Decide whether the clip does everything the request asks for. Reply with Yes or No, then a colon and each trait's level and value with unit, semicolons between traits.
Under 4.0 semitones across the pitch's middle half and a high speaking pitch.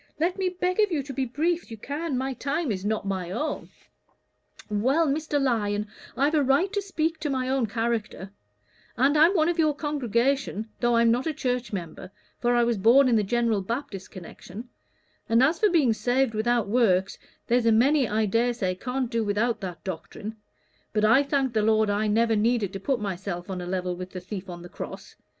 No: average, 5.2 semitones; high, 235 Hz